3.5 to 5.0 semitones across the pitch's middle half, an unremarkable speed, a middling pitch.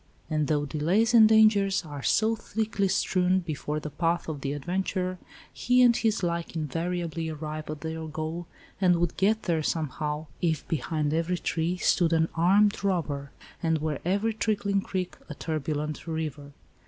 Yes: average, 3.8 semitones; average, 160 wpm; medium, 165 Hz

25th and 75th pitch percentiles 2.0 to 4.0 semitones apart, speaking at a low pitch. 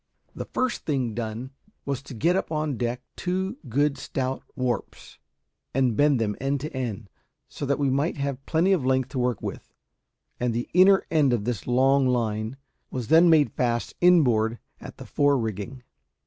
Yes: average, 3.6 semitones; low, 130 Hz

